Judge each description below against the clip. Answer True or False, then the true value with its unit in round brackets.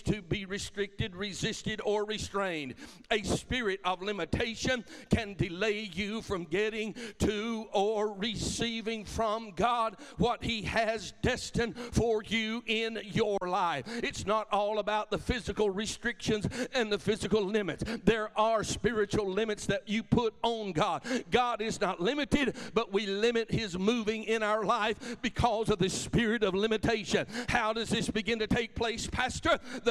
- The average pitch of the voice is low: False (215 Hz)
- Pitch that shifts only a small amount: True (1.8 semitones)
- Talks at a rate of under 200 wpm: True (155 wpm)